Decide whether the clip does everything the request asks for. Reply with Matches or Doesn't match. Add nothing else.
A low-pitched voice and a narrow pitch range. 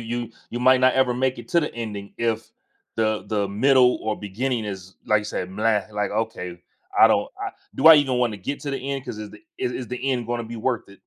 Doesn't match